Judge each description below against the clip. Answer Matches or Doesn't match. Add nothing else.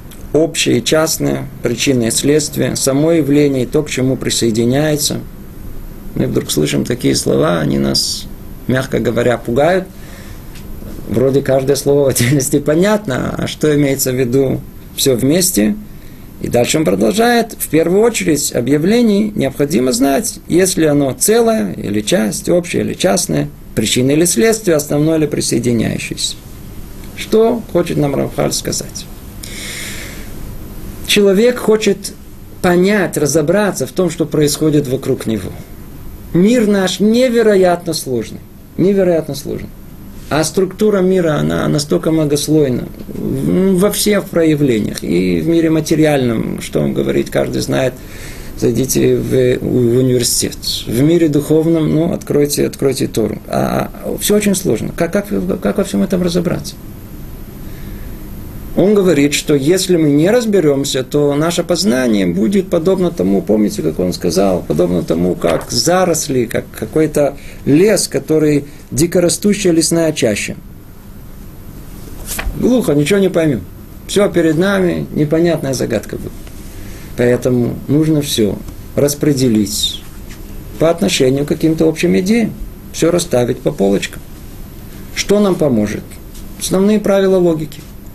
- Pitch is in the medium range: Matches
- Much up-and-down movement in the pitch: Matches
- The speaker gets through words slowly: Doesn't match